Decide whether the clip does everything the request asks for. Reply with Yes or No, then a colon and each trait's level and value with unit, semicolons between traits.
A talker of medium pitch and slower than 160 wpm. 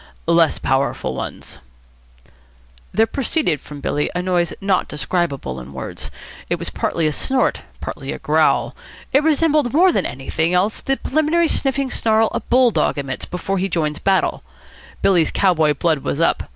No: medium, 180 Hz; average, 165 wpm